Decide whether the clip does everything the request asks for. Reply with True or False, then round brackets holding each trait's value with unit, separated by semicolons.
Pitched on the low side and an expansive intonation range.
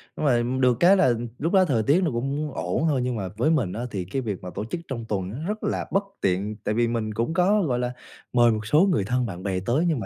True (120 Hz; 6.2 semitones)